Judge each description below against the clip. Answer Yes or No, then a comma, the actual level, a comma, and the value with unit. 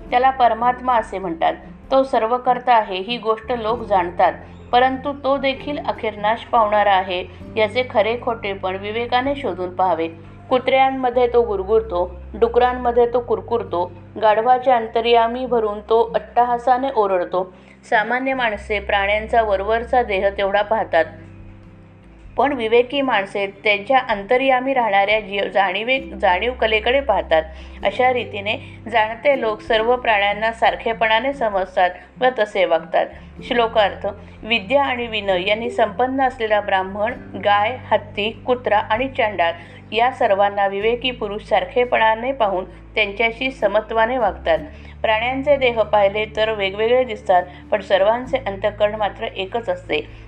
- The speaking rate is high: No, average, 120 wpm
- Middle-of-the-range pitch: No, high, 220 Hz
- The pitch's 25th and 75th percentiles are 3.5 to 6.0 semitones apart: Yes, average, 3.8 semitones